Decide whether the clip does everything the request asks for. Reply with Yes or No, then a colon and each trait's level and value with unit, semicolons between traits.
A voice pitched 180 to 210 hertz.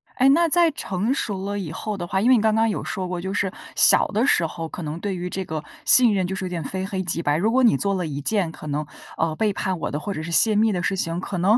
Yes: high, 190 Hz